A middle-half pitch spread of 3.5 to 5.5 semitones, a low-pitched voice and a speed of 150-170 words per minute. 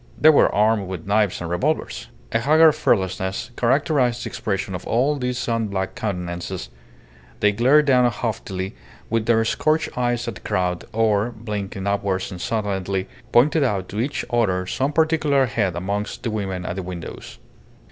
Yes: average, 4.7 semitones; low, 110 Hz; average, 160 wpm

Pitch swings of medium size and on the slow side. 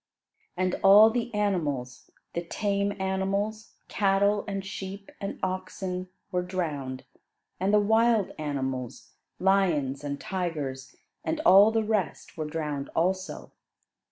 Yes: average, 4.9 semitones; slow, 120 wpm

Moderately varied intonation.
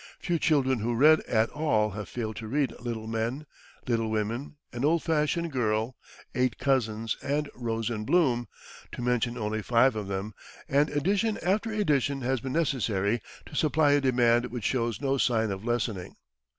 Yes: average, 4.5 semitones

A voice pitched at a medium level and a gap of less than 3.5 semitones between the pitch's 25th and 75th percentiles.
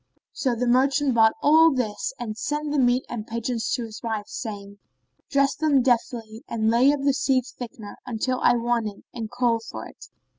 No: high, 240 Hz; average, 3.0 semitones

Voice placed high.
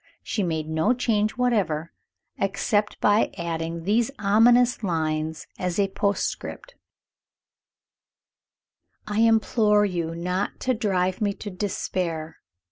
Yes: high, 200 Hz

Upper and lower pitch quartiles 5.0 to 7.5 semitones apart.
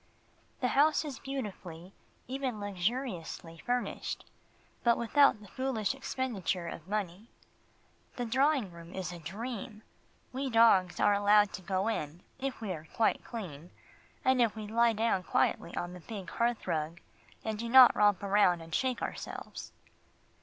Yes: average, 5.3 semitones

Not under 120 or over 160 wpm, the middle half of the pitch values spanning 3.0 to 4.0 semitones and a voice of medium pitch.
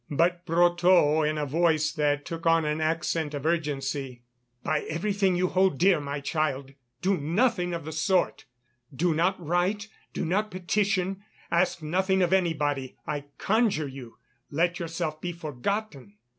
Yes: average, 150 wpm; average, 3.5 semitones; medium, 165 Hz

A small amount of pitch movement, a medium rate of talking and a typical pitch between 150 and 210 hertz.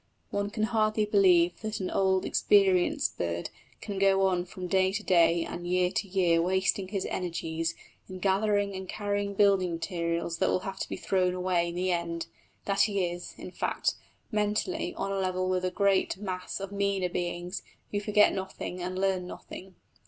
Yes: narrow, 2.0 semitones; average, 180 wpm; high, 190 Hz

